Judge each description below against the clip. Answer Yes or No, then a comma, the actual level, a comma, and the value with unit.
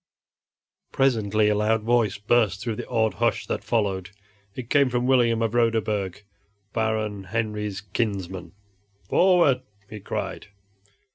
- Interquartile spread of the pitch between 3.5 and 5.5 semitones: No, narrow, 2.5 semitones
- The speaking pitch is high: No, low, 110 Hz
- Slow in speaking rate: Yes, slow, 125 wpm